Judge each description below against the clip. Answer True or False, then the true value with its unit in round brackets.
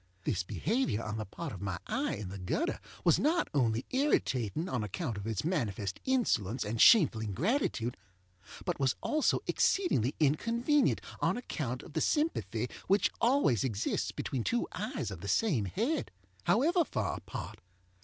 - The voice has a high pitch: False (135 Hz)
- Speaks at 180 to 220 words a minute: False (155 wpm)